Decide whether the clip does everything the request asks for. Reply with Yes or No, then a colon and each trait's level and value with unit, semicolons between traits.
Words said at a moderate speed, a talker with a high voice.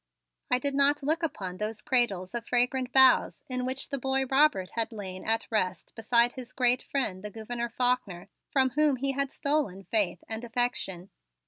Yes: average, 180 wpm; high, 245 Hz